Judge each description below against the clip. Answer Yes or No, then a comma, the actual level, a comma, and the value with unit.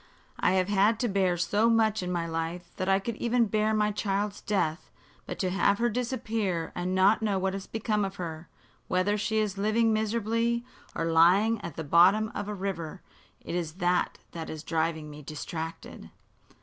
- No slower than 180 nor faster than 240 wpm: Yes, average, 190 wpm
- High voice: Yes, high, 195 Hz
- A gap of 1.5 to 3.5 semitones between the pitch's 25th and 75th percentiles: No, average, 3.9 semitones